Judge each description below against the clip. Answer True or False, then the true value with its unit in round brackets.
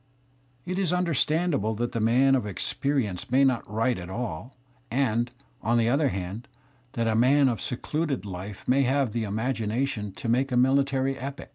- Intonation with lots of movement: False (3.7 semitones)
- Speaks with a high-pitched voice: False (125 Hz)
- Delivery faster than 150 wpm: True (170 wpm)